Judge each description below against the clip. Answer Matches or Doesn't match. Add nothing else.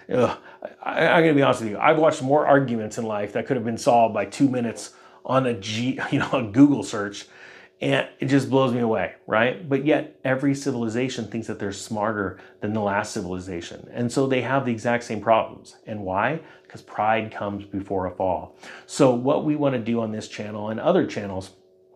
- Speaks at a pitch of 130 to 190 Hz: Doesn't match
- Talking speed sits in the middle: Doesn't match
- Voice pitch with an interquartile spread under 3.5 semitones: Doesn't match